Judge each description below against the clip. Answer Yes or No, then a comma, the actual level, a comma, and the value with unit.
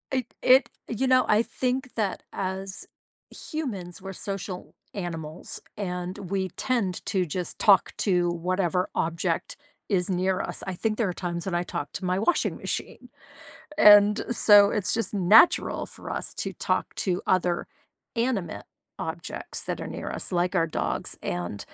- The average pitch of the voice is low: No, high, 190 Hz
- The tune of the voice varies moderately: Yes, average, 3.1 semitones